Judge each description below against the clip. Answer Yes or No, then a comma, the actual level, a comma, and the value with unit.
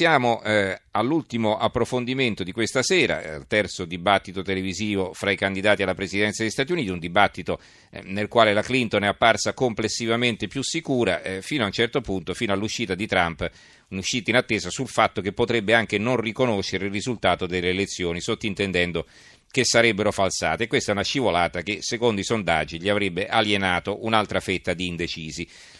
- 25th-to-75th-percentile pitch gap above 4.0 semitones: No, average, 3.5 semitones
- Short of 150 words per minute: No, average, 165 wpm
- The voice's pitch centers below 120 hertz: Yes, low, 105 Hz